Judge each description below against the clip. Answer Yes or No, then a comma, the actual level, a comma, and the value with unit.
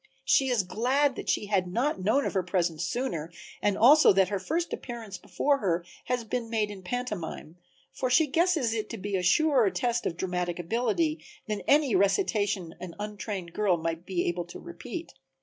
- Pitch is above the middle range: Yes, high, 210 Hz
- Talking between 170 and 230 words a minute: Yes, average, 190 wpm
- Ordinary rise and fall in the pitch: No, wide, 5.7 semitones